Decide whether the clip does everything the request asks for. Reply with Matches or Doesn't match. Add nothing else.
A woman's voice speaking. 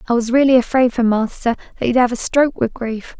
Matches